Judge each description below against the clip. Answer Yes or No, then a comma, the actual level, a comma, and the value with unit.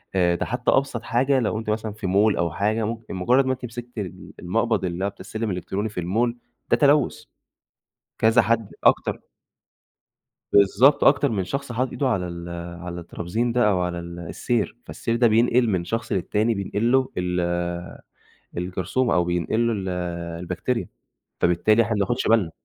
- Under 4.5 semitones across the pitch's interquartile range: No, average, 4.8 semitones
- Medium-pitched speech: No, low, 110 Hz